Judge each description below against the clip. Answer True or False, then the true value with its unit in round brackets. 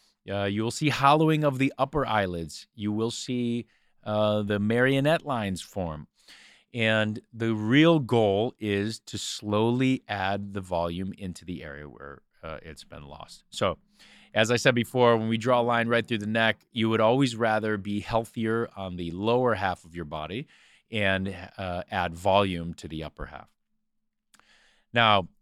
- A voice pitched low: True (110 Hz)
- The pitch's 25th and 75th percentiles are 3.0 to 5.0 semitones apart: True (4.2 semitones)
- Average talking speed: True (170 wpm)